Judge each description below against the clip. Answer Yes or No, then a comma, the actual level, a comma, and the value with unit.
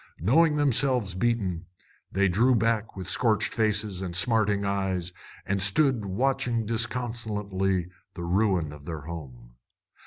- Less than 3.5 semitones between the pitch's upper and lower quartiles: No, average, 4.1 semitones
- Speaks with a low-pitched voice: Yes, low, 100 Hz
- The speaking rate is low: Yes, slow, 125 wpm